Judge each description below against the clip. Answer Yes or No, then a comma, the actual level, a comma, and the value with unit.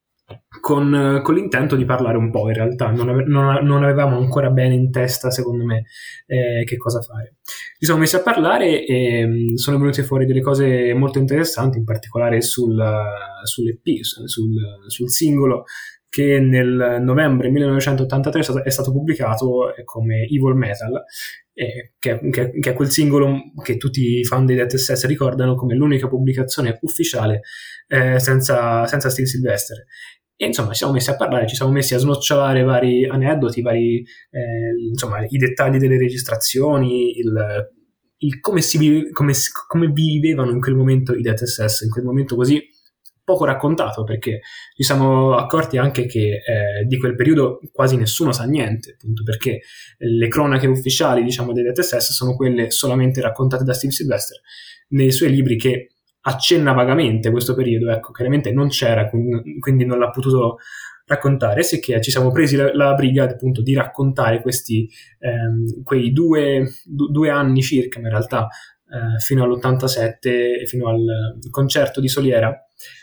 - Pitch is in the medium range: No, low, 130 Hz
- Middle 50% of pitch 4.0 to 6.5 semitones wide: No, narrow, 2.6 semitones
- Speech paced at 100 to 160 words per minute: Yes, average, 155 wpm